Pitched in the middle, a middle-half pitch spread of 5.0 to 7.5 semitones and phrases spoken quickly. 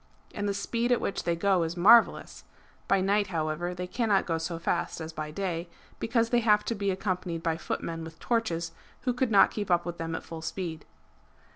No: medium, 180 Hz; average, 4.0 semitones; fast, 210 wpm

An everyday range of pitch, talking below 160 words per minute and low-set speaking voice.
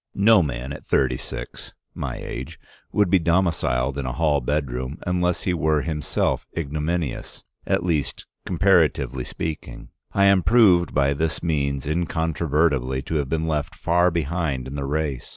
Yes: average, 3.7 semitones; average, 150 wpm; very low, 80 Hz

